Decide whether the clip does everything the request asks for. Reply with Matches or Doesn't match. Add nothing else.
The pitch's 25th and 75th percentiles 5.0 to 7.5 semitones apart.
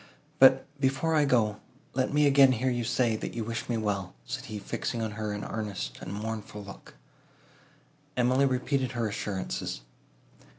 Doesn't match